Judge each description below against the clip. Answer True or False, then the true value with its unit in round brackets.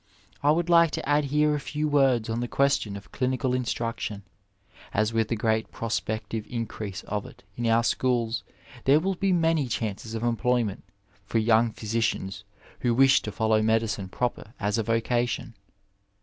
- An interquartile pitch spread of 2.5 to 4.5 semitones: True (3.4 semitones)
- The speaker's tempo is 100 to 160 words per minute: False (170 wpm)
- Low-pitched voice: True (115 Hz)